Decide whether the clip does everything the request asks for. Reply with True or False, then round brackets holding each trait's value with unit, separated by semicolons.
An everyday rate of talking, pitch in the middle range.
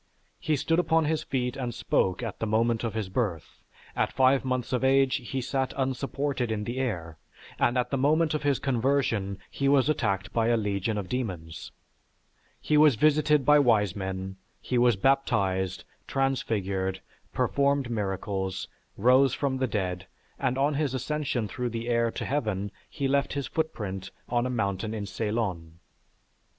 False (165 wpm; 120 Hz)